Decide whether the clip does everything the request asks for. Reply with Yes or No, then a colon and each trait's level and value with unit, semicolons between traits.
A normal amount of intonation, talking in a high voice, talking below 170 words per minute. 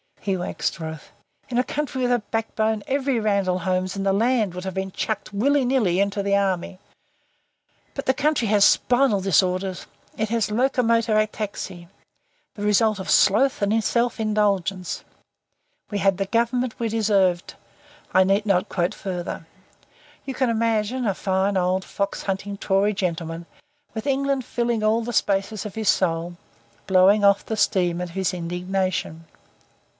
Yes: average, 3.4 semitones; high, 200 Hz; average, 155 wpm